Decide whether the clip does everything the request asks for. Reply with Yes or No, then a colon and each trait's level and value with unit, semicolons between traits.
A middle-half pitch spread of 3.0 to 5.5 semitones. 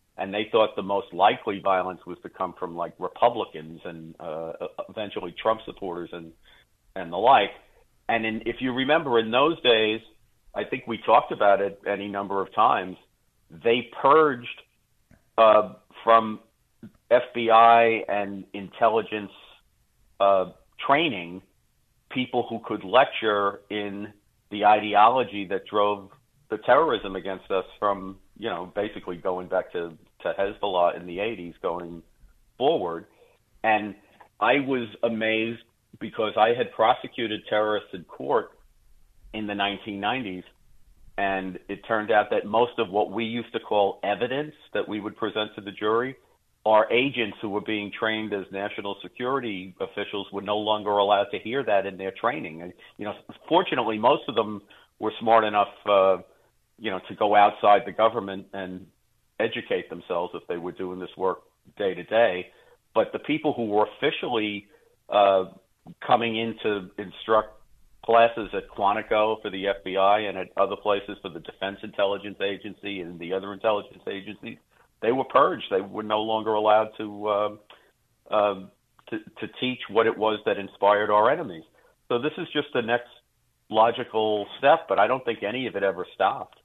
No: narrow, 2.4 semitones